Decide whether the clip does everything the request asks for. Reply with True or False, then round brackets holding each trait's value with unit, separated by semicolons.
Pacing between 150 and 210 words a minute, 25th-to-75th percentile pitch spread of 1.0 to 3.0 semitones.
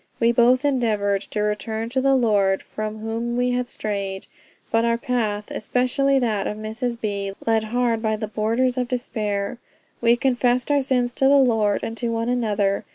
True (180 wpm; 2.7 semitones)